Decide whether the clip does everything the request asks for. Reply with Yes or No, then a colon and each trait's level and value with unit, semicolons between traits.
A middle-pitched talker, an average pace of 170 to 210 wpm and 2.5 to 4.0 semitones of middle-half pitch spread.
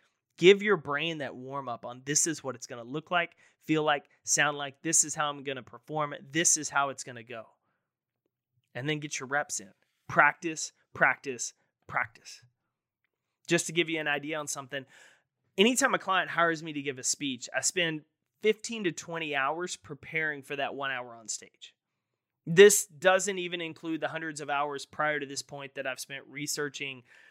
Yes: medium, 150 Hz; average, 190 wpm; average, 3.3 semitones